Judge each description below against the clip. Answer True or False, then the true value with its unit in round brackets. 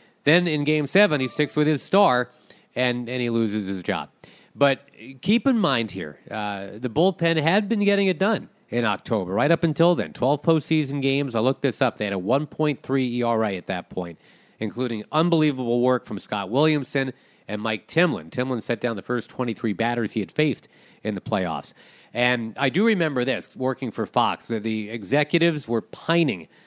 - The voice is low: True (130 Hz)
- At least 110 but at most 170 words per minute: False (190 wpm)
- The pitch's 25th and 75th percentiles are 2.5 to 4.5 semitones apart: False (5.2 semitones)